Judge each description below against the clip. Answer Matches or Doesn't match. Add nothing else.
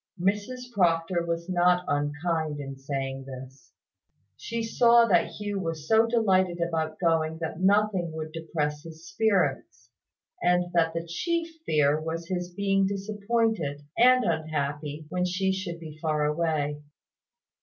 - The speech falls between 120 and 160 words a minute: Matches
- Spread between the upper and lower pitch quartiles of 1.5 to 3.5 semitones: Doesn't match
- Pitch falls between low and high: Matches